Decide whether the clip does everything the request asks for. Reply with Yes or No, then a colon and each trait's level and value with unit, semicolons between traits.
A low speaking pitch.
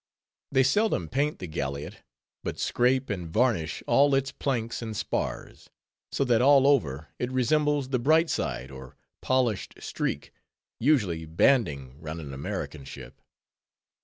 Yes: low, 120 Hz